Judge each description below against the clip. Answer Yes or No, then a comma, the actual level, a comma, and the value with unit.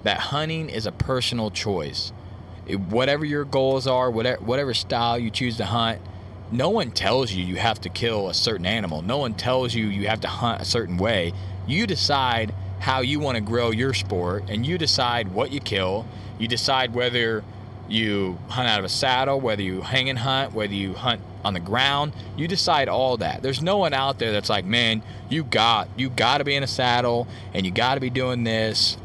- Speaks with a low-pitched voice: Yes, low, 115 Hz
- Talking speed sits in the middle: No, fast, 215 wpm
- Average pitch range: Yes, average, 4.0 semitones